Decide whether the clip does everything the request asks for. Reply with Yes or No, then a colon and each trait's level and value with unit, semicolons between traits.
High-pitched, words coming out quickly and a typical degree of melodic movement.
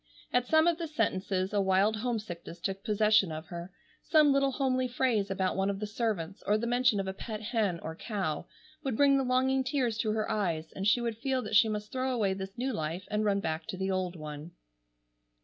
Yes: high, 210 Hz; fast, 220 wpm; average, 4.7 semitones